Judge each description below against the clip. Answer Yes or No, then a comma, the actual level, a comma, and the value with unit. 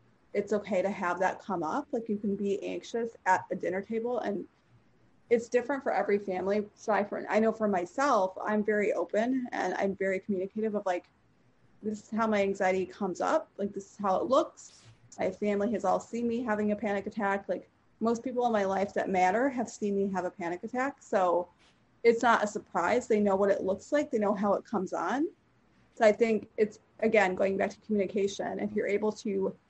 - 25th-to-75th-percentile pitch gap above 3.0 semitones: No, average, 2.7 semitones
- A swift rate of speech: Yes, fast, 215 wpm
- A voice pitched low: No, high, 205 Hz